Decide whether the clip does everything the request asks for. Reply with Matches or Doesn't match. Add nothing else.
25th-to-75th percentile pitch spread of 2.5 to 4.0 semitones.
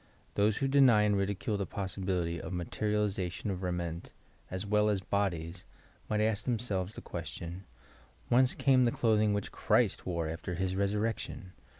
Matches